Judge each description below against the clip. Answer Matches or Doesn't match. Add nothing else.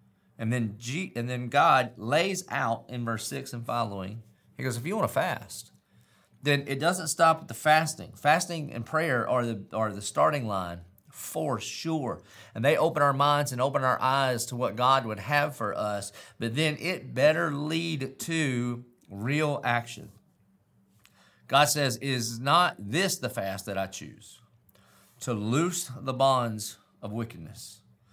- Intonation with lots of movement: Doesn't match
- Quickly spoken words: Doesn't match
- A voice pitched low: Matches